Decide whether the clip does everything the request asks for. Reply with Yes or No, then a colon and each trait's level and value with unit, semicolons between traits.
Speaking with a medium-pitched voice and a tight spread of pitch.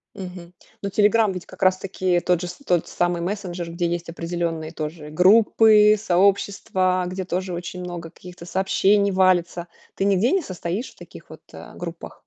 Yes: medium, 180 Hz; narrow, 2.3 semitones